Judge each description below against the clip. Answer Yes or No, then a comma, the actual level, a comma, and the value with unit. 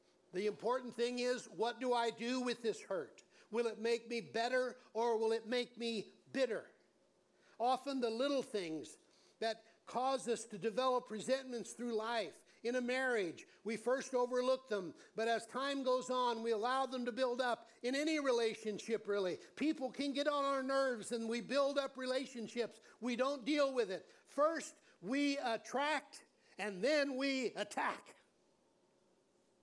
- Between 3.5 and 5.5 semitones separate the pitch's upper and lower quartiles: No, average, 2.7 semitones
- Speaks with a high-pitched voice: Yes, high, 245 Hz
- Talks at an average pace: Yes, average, 160 wpm